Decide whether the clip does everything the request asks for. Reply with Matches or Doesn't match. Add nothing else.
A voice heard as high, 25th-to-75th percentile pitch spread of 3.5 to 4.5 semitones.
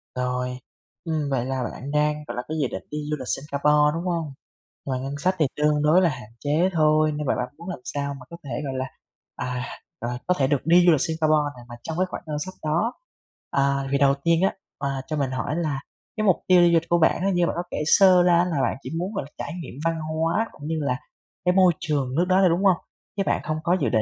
Doesn't match